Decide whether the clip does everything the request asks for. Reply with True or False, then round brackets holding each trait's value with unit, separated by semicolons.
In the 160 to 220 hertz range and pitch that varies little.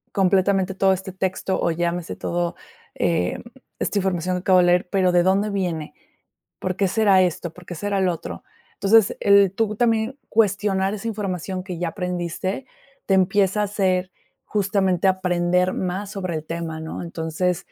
True (185 Hz; 2.0 semitones)